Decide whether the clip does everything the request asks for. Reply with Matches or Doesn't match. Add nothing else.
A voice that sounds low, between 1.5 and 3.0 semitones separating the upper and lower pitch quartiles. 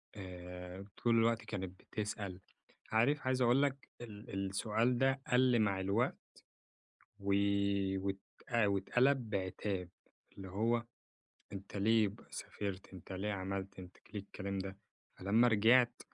Doesn't match